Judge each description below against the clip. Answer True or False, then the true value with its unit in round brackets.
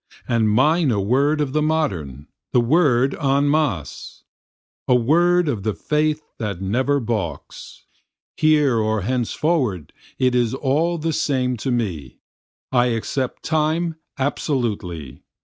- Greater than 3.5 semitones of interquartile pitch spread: True (5.6 semitones)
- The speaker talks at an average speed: False (130 wpm)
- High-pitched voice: False (130 Hz)